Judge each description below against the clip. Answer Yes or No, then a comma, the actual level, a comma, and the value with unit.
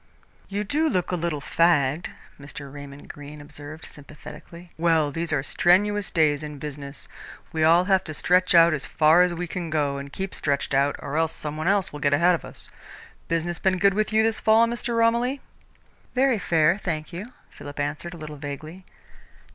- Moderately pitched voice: Yes, medium, 165 Hz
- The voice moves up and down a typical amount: Yes, average, 4.1 semitones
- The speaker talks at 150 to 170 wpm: No, average, 190 wpm